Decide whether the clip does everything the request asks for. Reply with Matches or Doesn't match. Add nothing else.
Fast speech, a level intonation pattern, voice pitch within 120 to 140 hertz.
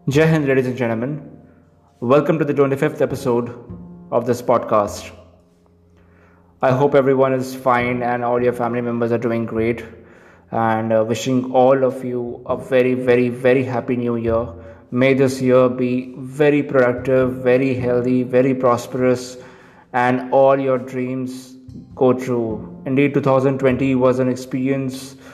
Doesn't match